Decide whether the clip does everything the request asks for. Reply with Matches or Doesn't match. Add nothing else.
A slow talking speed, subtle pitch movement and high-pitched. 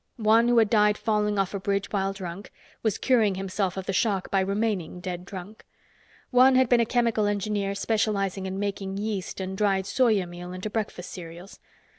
Doesn't match